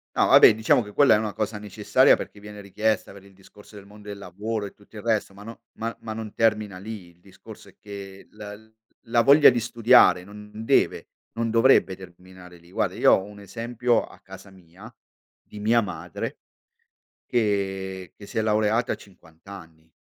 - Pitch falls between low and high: No, low, 105 Hz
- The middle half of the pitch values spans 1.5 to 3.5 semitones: Yes, narrow, 2.5 semitones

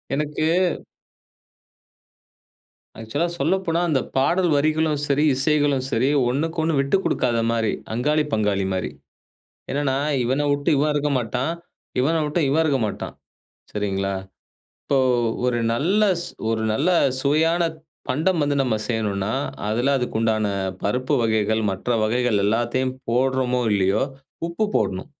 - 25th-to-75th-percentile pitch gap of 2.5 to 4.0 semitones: No, average, 5.1 semitones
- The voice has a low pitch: Yes, low, 130 Hz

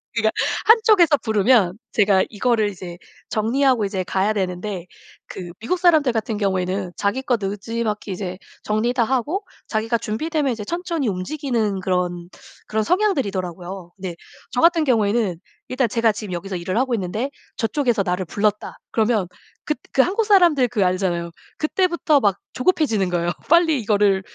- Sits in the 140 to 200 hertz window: No, high, 215 Hz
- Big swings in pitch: Yes, wide, 5.7 semitones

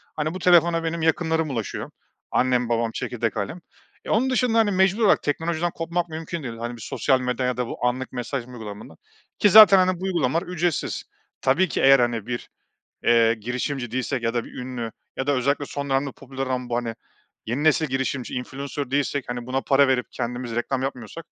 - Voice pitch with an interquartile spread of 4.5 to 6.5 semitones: Yes, average, 4.9 semitones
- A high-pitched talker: No, low, 135 Hz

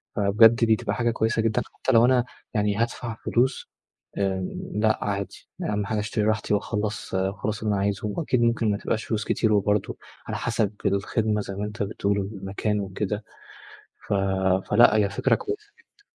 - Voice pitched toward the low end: Yes, low, 105 Hz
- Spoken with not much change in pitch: Yes, narrow, 2.0 semitones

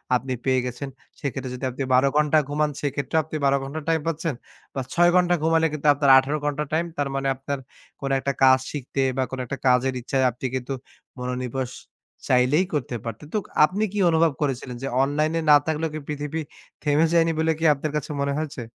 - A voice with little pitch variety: No, average, 3.1 semitones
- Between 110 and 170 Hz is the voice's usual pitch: Yes, medium, 140 Hz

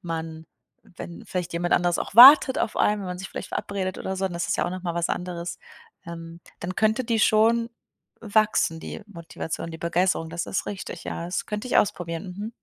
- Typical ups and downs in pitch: Yes, average, 3.6 semitones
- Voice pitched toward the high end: No, medium, 180 Hz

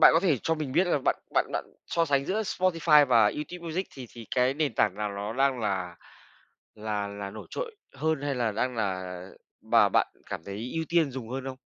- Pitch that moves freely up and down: Yes, wide, 6.9 semitones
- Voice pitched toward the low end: Yes, low, 130 Hz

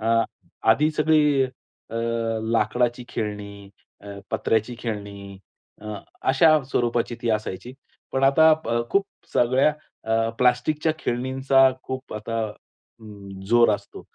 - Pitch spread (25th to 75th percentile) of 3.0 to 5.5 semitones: Yes, average, 3.8 semitones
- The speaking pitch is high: No, low, 120 Hz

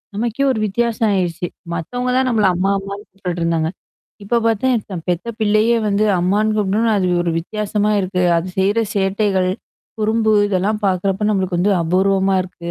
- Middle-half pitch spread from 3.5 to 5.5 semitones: No, average, 2.8 semitones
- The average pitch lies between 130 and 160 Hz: No, high, 200 Hz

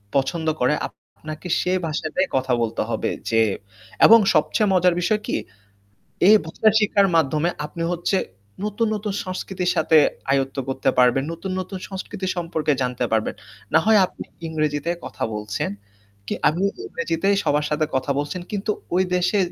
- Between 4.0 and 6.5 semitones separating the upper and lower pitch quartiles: Yes, average, 4.7 semitones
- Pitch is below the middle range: No, medium, 165 Hz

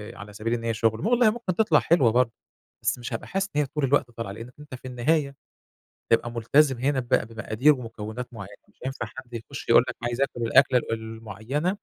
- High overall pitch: No, low, 120 Hz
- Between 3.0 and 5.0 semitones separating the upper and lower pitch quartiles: Yes, average, 3.7 semitones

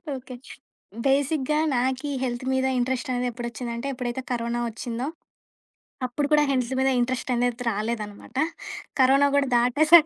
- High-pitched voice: Yes, very high, 250 Hz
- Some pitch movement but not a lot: No, narrow, 1.9 semitones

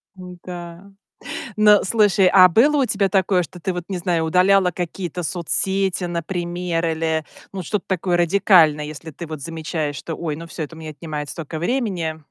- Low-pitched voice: No, medium, 175 Hz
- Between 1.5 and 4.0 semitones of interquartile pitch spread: Yes, average, 2.9 semitones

